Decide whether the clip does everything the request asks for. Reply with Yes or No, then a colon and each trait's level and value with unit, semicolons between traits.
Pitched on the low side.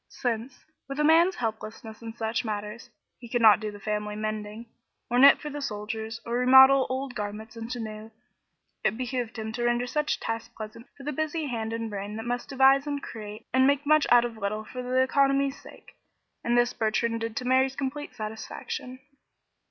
No: high, 235 Hz